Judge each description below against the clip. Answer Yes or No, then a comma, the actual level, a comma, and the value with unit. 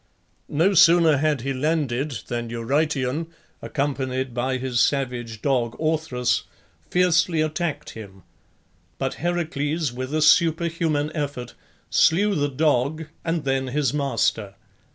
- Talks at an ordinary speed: No, slow, 115 wpm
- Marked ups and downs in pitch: No, average, 4.0 semitones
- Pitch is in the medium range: Yes, medium, 145 Hz